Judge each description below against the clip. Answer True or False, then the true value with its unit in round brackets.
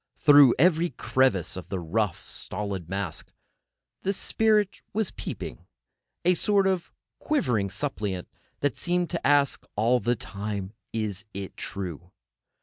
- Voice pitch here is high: False (115 Hz)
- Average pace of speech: False (130 wpm)